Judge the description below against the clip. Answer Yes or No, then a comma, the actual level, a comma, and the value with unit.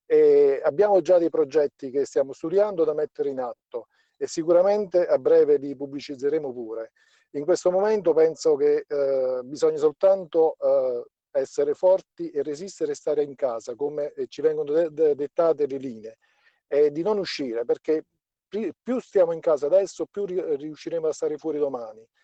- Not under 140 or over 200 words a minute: Yes, average, 155 wpm